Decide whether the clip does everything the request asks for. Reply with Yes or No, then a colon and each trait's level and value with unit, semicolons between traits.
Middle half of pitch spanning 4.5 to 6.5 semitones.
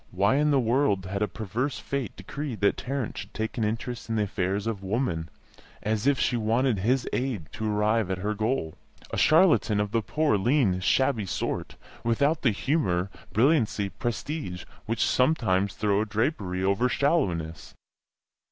Yes: average, 4.9 semitones